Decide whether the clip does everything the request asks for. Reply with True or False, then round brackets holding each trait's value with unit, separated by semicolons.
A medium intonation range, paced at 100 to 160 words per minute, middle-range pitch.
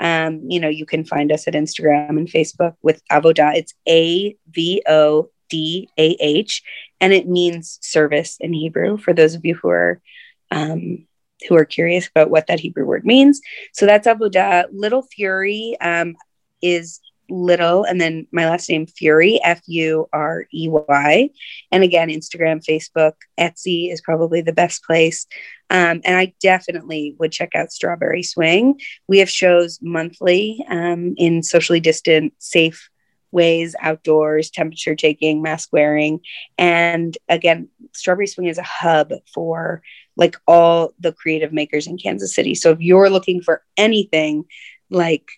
False (2.2 semitones; 150 wpm; 165 Hz)